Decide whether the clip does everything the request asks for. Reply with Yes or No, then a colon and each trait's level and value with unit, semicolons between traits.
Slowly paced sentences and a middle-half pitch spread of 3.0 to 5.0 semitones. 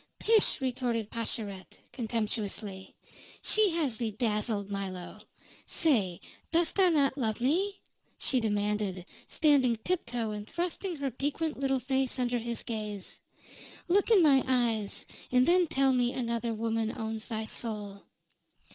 Yes: slow, 130 wpm; average, 4.5 semitones